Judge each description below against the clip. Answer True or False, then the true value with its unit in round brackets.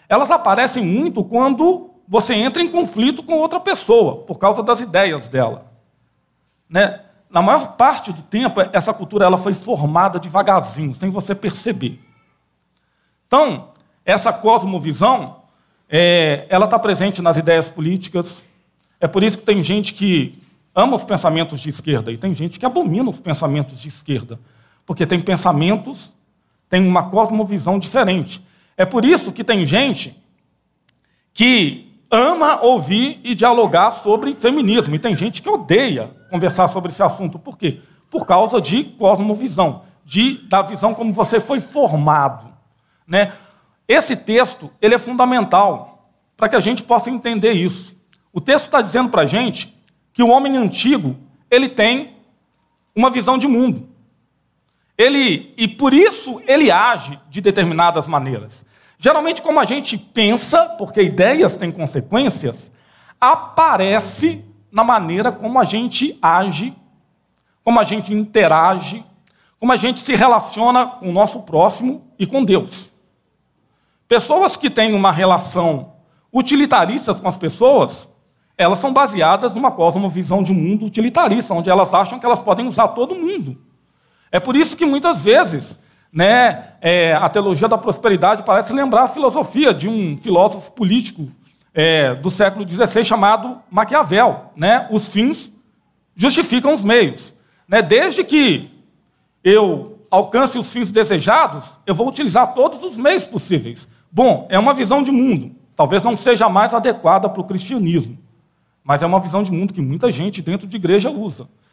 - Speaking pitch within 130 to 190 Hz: False (210 Hz)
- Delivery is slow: False (150 wpm)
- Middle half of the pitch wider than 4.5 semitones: True (5.5 semitones)